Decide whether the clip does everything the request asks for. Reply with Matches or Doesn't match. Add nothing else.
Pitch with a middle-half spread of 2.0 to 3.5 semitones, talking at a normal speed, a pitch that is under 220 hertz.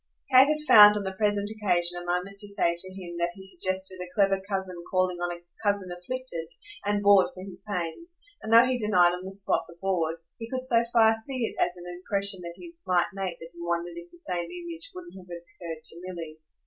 Doesn't match